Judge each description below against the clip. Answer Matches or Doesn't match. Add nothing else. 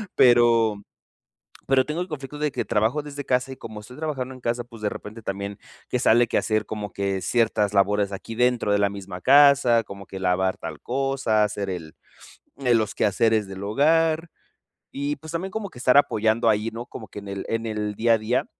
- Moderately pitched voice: Doesn't match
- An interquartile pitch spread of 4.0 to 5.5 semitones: Matches